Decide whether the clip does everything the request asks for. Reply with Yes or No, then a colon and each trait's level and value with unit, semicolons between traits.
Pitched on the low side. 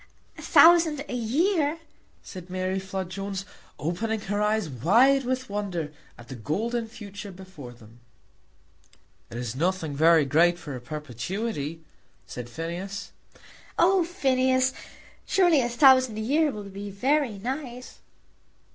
No: high, 200 Hz